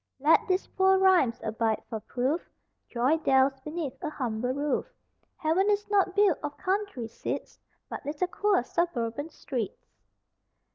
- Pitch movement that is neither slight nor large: No, wide, 6.9 semitones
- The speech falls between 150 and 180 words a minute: No, average, 140 wpm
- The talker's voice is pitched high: Yes, very high, 295 Hz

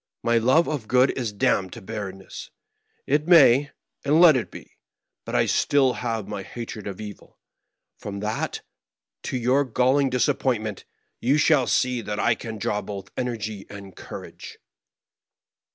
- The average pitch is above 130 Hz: No, low, 115 Hz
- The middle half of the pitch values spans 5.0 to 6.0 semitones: No, average, 4.1 semitones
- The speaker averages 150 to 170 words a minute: Yes, average, 160 wpm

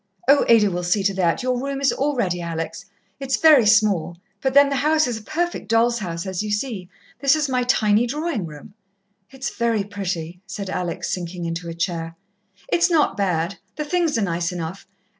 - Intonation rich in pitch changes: Yes, wide, 7.3 semitones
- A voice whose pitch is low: No, high, 210 Hz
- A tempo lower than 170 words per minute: No, average, 195 wpm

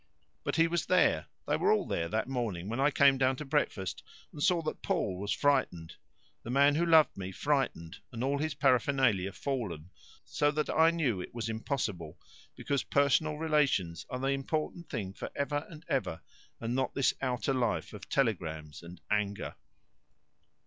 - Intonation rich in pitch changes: Yes, wide, 6.6 semitones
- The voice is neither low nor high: No, low, 130 Hz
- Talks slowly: No, average, 175 wpm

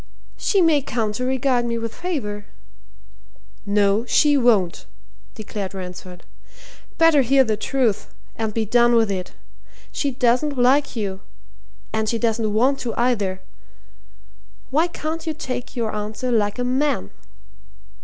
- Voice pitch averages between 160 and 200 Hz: No, high, 235 Hz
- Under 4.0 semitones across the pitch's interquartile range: No, average, 4.4 semitones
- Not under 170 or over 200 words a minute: No, slow, 135 wpm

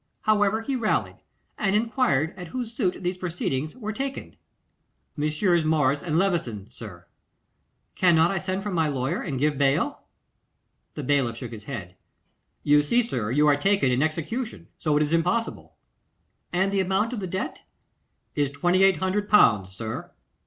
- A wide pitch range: Yes, wide, 5.7 semitones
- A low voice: No, medium, 170 Hz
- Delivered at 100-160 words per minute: Yes, average, 150 wpm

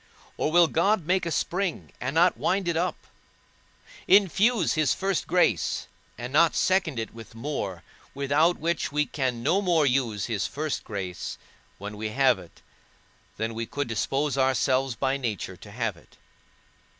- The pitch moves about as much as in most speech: No, wide, 6.8 semitones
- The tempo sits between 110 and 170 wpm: Yes, average, 160 wpm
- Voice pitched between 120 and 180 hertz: Yes, medium, 140 Hz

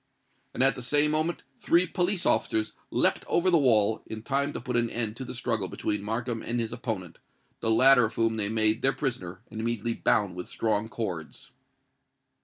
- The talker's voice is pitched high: No, low, 115 Hz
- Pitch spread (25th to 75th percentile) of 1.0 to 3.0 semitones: No, average, 3.6 semitones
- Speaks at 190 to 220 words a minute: Yes, average, 195 wpm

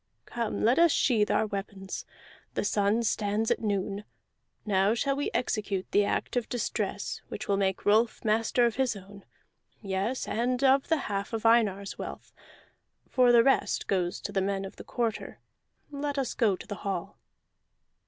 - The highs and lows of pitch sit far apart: No, average, 3.3 semitones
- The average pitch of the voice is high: Yes, high, 215 Hz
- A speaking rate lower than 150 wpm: No, average, 170 wpm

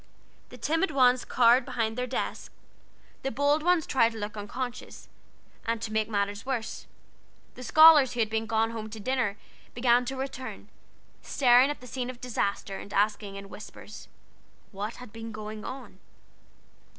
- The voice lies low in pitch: No, high, 235 Hz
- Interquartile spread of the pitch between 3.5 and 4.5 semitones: No, average, 3.0 semitones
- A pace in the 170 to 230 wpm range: No, average, 160 wpm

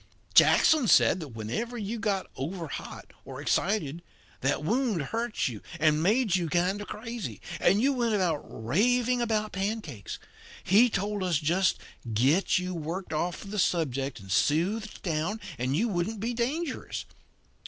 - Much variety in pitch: Yes, wide, 6.4 semitones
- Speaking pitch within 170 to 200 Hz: Yes, high, 190 Hz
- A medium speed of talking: Yes, average, 155 wpm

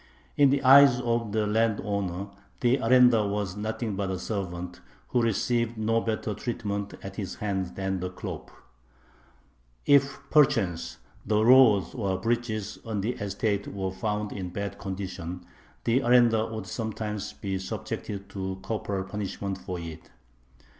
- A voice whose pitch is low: Yes, low, 105 Hz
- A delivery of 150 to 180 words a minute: No, average, 140 wpm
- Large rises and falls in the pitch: No, average, 3.0 semitones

